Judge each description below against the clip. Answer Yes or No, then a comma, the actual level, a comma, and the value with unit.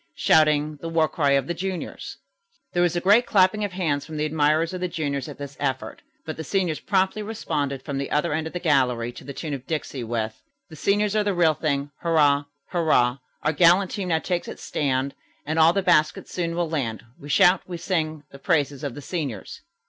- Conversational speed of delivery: No, fast, 215 wpm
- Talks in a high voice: No, medium, 155 Hz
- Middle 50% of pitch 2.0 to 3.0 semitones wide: No, average, 3.8 semitones